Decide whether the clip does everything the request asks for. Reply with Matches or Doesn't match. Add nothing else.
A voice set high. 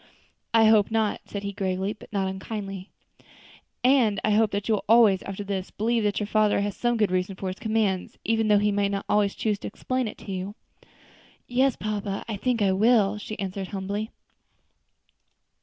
Matches